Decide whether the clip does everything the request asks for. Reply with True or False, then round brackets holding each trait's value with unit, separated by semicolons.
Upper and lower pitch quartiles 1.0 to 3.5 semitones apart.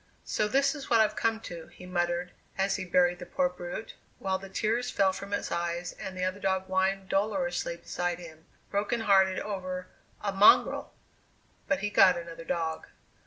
True (2.6 semitones)